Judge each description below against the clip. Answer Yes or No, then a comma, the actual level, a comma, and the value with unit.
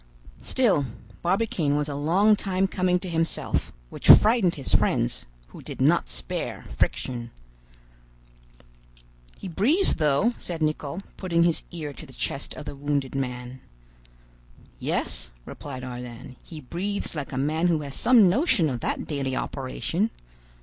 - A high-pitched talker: No, medium, 155 Hz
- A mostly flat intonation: No, wide, 5.4 semitones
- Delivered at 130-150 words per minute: Yes, average, 145 wpm